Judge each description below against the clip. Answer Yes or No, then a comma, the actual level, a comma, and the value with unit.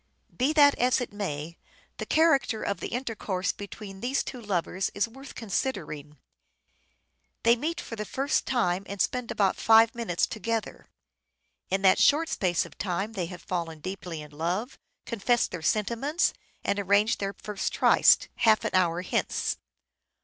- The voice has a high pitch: Yes, high, 205 Hz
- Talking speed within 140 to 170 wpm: Yes, average, 160 wpm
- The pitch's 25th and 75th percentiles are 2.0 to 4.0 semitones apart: No, average, 4.8 semitones